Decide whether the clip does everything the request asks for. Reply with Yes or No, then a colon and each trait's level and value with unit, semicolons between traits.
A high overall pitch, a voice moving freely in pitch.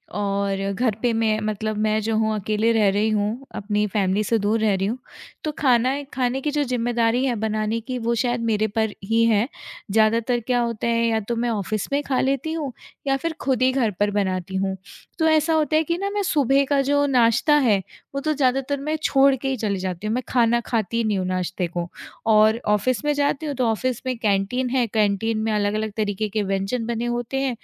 No: high, 230 Hz; average, 3.7 semitones